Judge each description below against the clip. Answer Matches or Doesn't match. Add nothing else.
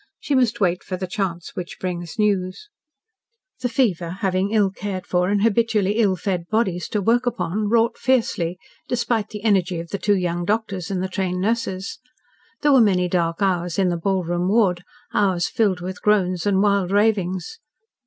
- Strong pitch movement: Doesn't match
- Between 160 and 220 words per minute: Matches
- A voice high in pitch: Matches